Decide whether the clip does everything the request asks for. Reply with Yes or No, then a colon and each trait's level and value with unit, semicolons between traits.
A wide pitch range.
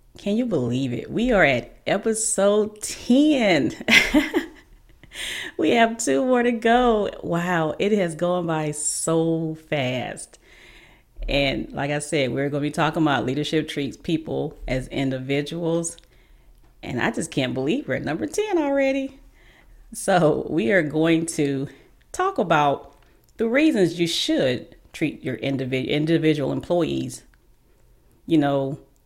Yes: wide, 7.5 semitones